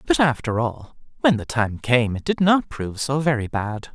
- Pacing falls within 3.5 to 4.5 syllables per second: No, 4.8 syllables/s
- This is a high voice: No, low, 130 Hz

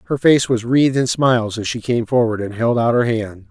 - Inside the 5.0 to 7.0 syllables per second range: Yes, 5.5 syllables/s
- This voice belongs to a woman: No, male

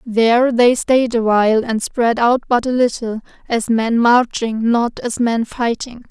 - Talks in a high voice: Yes, high, 235 Hz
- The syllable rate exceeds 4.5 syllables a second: No, 4.1 syllables/s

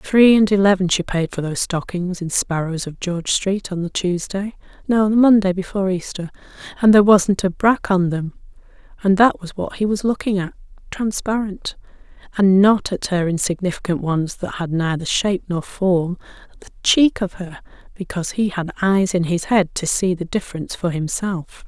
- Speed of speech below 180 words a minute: No, average, 185 wpm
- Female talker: Yes, female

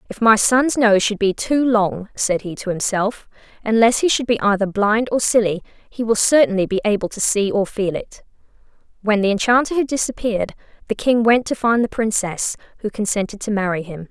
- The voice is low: No, high, 215 Hz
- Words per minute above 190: Yes, average, 200 wpm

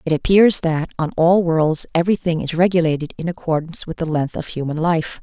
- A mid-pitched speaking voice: Yes, medium, 165 Hz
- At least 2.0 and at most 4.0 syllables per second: No, 5.8 syllables/s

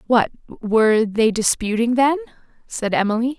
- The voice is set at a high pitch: Yes, high, 235 Hz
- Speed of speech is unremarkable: No, slow, 125 wpm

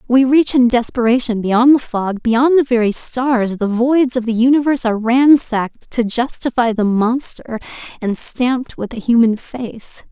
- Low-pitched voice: No, high, 240 Hz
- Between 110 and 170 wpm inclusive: Yes, average, 165 wpm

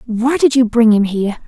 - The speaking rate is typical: No, fast, 245 wpm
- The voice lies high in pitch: Yes, high, 235 Hz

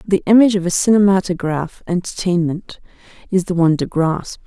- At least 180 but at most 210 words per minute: No, average, 150 wpm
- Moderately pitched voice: Yes, medium, 180 Hz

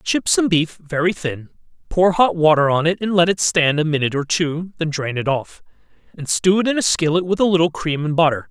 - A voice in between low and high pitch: Yes, medium, 165 Hz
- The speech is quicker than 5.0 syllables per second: Yes, 5.5 syllables/s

